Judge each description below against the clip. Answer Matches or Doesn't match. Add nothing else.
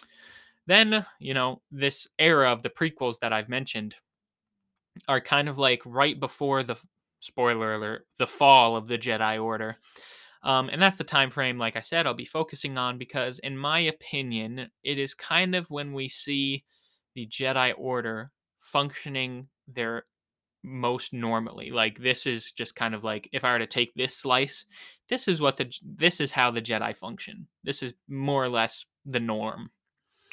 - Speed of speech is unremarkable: Matches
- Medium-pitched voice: Doesn't match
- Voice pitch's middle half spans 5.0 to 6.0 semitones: Doesn't match